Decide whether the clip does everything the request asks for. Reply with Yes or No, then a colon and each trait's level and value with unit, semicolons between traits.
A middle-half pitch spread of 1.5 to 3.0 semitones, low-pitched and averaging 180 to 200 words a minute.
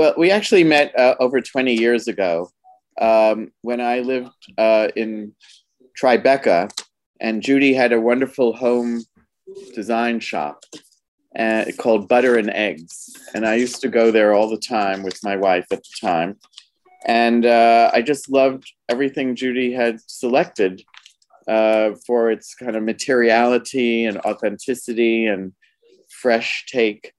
No: average, 2.7 semitones; low, 120 Hz; average, 140 wpm